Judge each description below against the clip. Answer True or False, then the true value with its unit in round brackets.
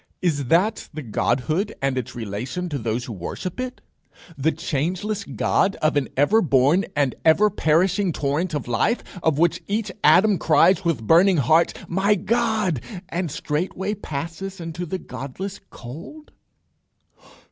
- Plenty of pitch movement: True (5.7 semitones)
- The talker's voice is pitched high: False (165 Hz)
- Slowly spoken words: False (145 wpm)